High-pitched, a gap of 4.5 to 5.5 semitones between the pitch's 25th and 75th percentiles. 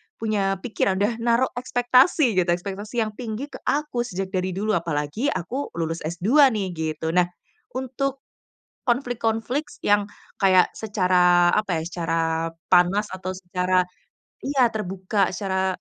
Yes: high, 200 Hz; average, 4.9 semitones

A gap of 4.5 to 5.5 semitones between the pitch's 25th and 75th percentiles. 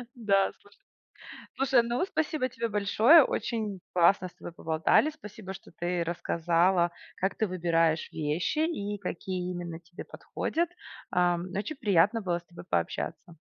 Yes: average, 4.8 semitones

